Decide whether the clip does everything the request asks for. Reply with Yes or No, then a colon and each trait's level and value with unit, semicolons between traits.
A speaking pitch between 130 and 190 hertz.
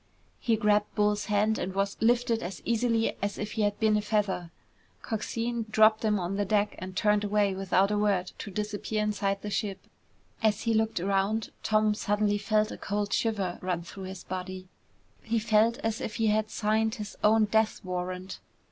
No: high, 210 Hz